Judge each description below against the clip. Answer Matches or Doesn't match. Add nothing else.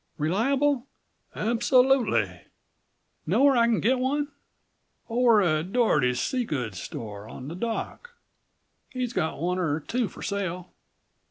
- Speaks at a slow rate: Matches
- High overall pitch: Matches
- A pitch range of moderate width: Doesn't match